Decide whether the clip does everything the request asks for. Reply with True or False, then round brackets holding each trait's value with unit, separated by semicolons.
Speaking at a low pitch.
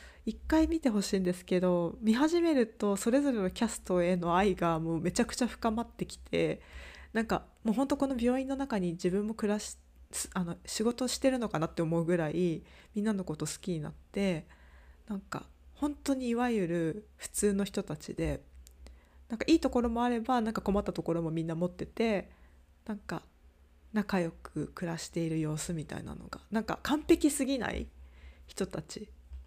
False (195 Hz)